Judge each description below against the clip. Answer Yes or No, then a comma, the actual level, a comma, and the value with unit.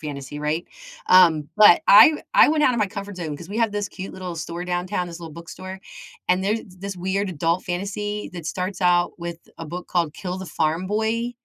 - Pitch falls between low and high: Yes, medium, 180 Hz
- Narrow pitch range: No, average, 3.1 semitones